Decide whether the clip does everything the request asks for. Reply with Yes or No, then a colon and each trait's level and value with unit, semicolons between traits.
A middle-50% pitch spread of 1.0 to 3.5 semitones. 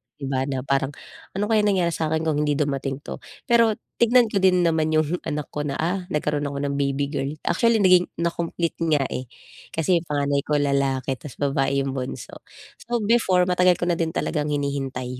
No: average, 4.4 semitones